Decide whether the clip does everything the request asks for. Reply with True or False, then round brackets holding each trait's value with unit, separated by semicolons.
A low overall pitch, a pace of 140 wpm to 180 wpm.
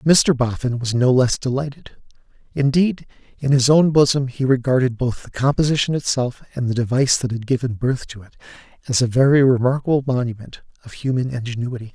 True (130 Hz; 170 wpm)